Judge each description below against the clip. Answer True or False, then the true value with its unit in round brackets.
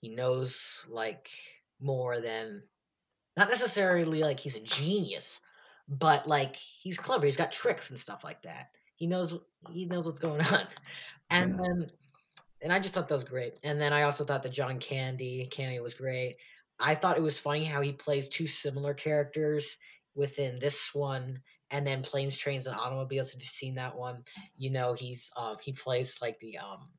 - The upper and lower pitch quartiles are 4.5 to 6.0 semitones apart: False (3.6 semitones)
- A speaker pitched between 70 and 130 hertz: False (140 Hz)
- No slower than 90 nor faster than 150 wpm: False (185 wpm)